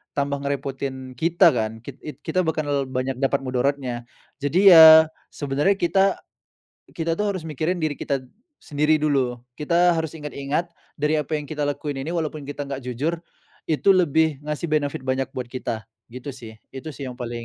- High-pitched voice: No, medium, 145 Hz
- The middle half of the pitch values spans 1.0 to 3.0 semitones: Yes, average, 2.7 semitones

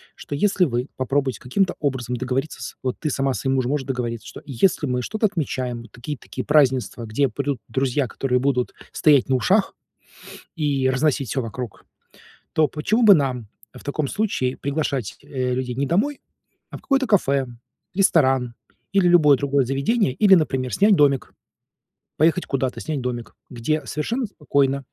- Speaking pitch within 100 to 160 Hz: Yes, low, 135 Hz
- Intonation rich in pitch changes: No, average, 3.6 semitones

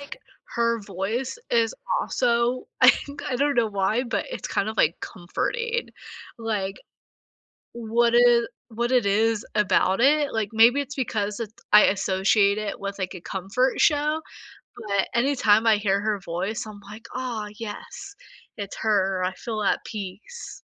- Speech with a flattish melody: No, average, 3.5 semitones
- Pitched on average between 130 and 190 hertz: No, high, 220 Hz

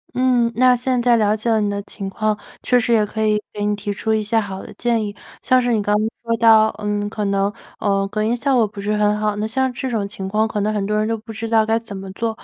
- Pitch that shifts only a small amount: Yes, narrow, 1.9 semitones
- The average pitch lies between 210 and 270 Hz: Yes, high, 215 Hz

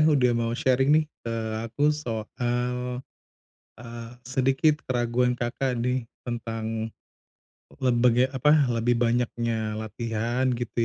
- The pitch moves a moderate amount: No, narrow, 2.0 semitones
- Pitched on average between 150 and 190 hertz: No, low, 120 Hz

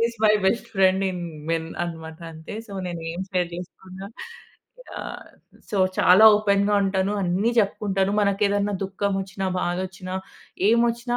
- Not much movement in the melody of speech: Yes, narrow, 2.1 semitones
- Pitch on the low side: No, high, 195 Hz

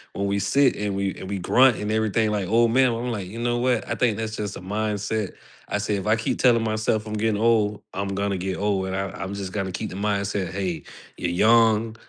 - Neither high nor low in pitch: No, low, 105 Hz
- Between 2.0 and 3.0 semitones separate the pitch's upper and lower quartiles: Yes, narrow, 2.4 semitones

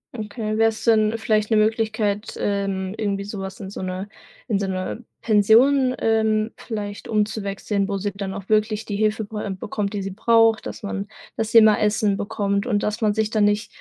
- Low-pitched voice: No, high, 210 Hz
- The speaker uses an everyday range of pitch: No, narrow, 1.6 semitones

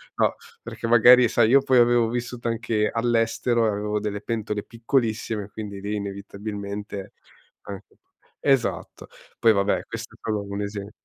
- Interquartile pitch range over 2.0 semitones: Yes, narrow, 2.4 semitones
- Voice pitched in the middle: No, low, 110 Hz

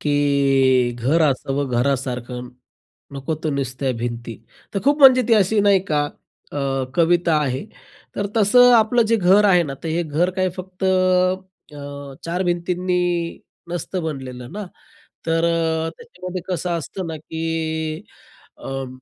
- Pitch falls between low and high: Yes, medium, 165 Hz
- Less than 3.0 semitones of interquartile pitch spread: No, average, 5.3 semitones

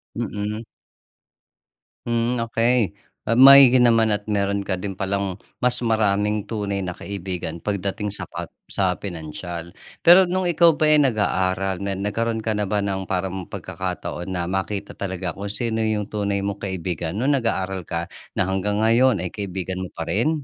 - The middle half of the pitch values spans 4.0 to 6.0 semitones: No, average, 3.3 semitones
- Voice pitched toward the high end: No, low, 100 Hz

